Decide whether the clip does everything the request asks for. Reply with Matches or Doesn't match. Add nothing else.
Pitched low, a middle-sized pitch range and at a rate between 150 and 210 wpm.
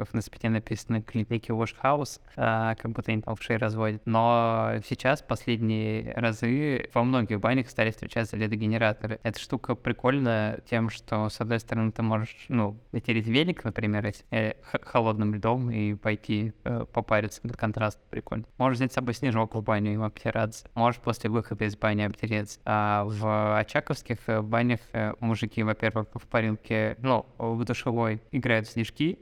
Doesn't match